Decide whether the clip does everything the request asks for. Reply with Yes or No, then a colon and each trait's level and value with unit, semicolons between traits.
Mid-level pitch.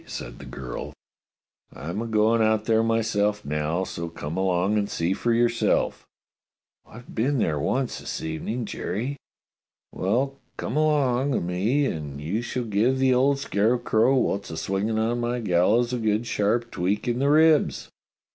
No: low, 110 Hz